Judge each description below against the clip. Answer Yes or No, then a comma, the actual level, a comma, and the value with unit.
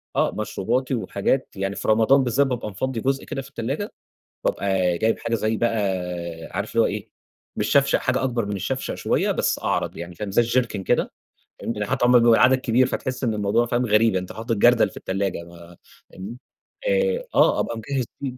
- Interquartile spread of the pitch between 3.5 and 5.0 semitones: Yes, average, 4.2 semitones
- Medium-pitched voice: No, low, 115 Hz